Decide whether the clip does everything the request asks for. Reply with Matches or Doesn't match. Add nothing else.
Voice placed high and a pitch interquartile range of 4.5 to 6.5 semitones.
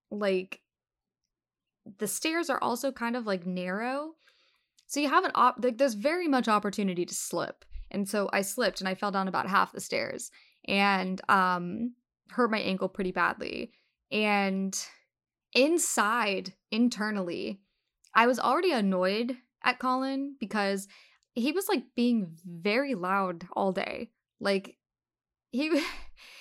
Matches